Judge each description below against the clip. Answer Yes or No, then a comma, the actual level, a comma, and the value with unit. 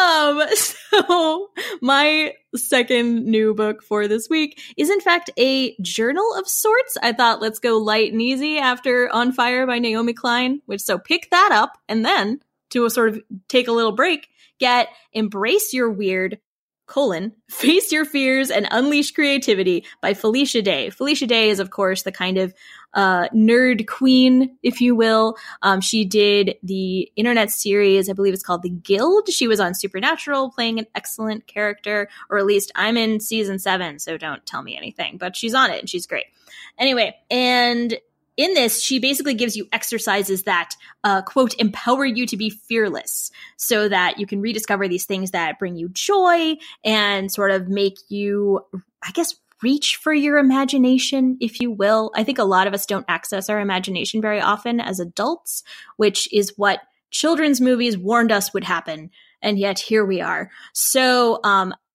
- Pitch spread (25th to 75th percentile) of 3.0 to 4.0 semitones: No, average, 4.6 semitones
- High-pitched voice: Yes, high, 225 Hz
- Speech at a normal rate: Yes, average, 175 wpm